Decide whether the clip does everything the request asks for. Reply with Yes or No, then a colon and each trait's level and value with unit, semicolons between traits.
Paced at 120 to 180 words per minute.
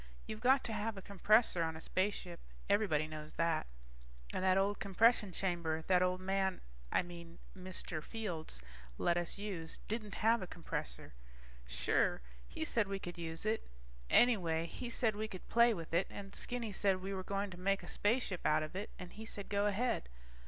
No: average, 190 wpm